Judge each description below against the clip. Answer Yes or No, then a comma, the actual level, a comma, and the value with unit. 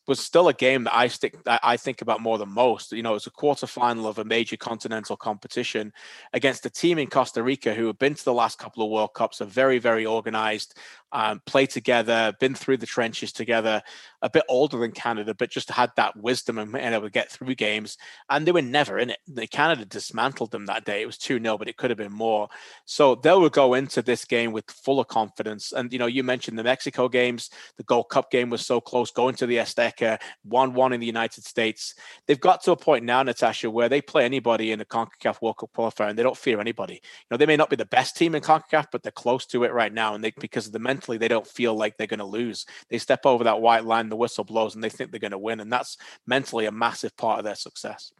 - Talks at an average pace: No, fast, 255 wpm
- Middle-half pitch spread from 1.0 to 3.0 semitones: Yes, average, 2.7 semitones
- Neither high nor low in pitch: No, low, 120 Hz